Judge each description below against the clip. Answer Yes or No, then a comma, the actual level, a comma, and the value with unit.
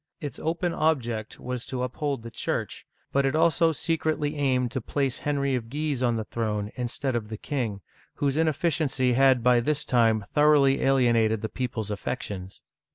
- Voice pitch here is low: Yes, low, 130 Hz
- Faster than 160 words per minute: Yes, average, 175 wpm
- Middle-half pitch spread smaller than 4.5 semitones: Yes, average, 4.1 semitones